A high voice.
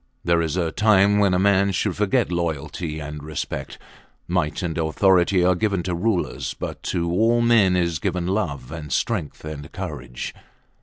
No: very low, 90 Hz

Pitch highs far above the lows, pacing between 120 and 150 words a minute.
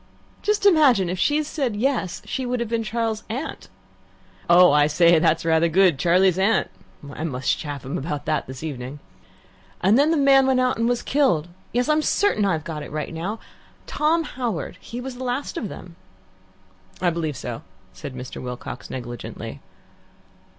No: wide, 8.3 semitones; average, 170 wpm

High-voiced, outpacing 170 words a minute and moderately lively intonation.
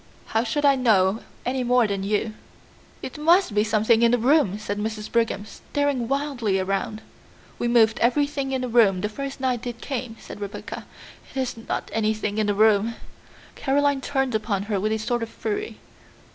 Yes: high, 230 Hz; average, 185 wpm; average, 3.8 semitones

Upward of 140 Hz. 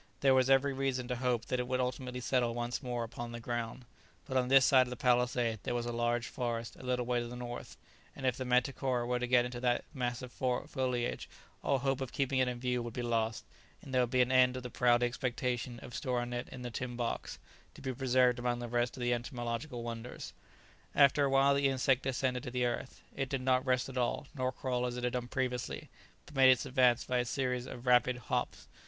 No: low, 125 Hz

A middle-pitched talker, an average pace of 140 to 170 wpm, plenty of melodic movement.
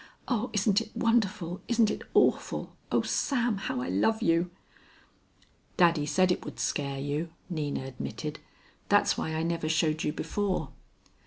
Yes: medium, 170 Hz; average, 150 wpm; wide, 5.8 semitones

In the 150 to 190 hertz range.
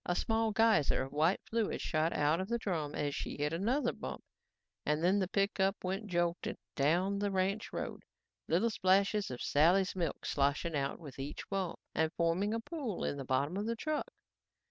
Yes: medium, 185 Hz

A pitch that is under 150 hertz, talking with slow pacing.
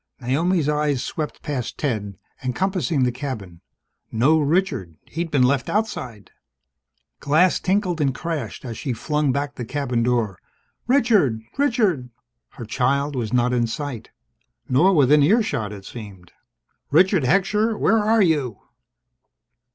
Yes: medium, 140 Hz; slow, 130 wpm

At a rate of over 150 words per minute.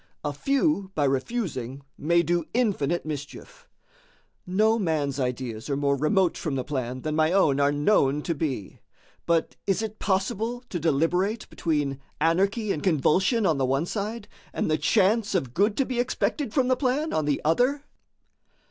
Yes: average, 165 wpm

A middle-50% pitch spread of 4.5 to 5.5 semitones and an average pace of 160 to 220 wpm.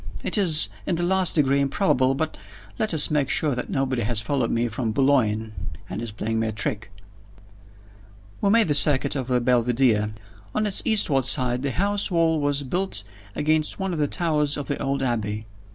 Yes: average, 5.1 semitones; average, 190 wpm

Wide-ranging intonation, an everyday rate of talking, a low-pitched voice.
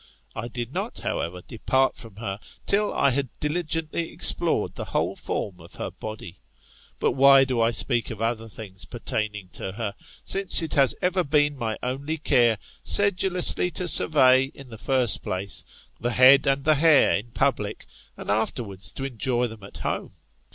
No: average, 4.5 semitones; average, 170 wpm; low, 125 Hz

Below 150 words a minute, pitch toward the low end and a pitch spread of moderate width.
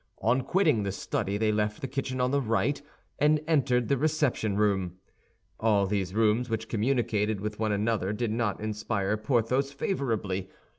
No: average, 160 wpm; low, 110 Hz; average, 3.8 semitones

